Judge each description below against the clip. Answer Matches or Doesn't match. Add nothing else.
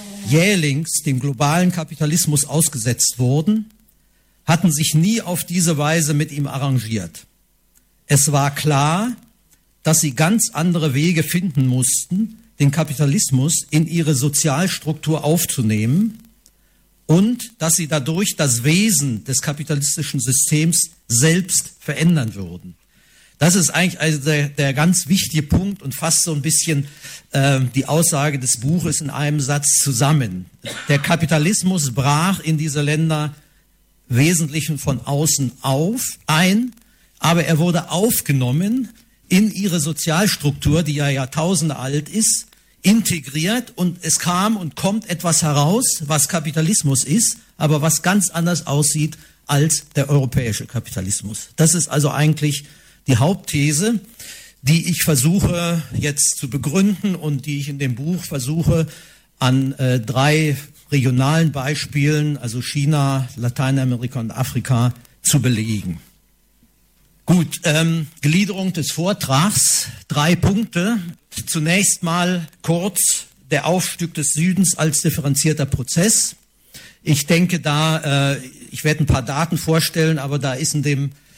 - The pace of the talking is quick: Doesn't match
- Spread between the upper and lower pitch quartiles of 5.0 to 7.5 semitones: Doesn't match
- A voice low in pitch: Doesn't match